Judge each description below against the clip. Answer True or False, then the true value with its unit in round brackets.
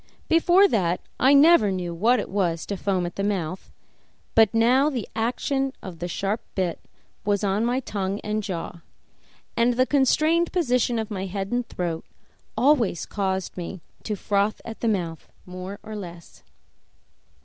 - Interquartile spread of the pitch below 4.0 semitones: False (4.9 semitones)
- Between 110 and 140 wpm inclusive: False (160 wpm)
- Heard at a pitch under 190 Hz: False (205 Hz)